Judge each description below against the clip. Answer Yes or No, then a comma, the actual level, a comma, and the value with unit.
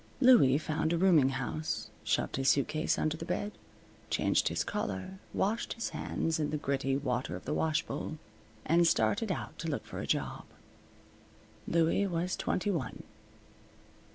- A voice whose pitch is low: No, medium, 160 Hz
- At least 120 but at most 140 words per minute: No, average, 155 wpm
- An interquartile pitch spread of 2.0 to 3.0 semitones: No, average, 4.8 semitones